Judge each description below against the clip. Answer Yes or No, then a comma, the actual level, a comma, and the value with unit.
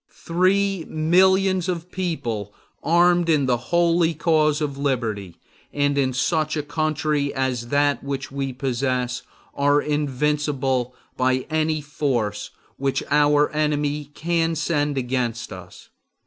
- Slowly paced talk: Yes, slow, 120 wpm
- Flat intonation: No, average, 3.4 semitones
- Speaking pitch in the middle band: Yes, medium, 145 Hz